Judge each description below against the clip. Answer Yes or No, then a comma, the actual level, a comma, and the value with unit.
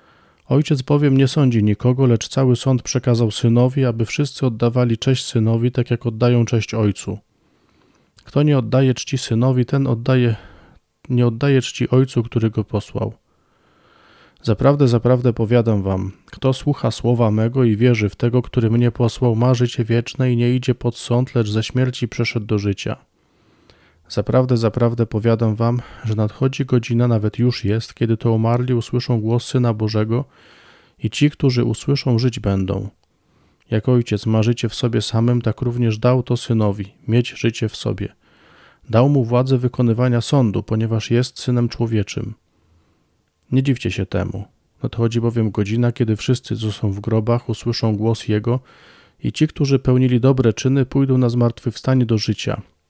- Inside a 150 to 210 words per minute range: Yes, average, 155 wpm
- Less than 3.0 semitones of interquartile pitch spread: Yes, narrow, 2.4 semitones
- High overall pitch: No, low, 120 Hz